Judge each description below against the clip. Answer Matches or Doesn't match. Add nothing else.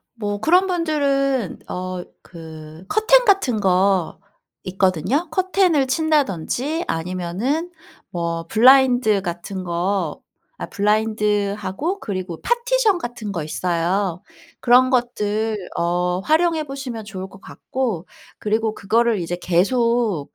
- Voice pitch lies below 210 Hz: Doesn't match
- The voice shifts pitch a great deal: Matches